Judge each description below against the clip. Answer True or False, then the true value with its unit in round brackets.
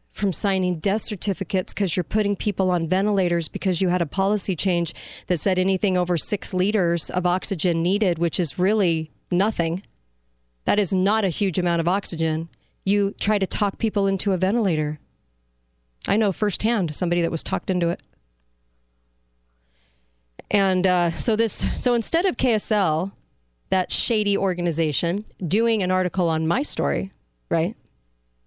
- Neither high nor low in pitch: True (180 Hz)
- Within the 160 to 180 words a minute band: False (150 wpm)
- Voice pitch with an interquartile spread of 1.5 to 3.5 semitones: False (4.0 semitones)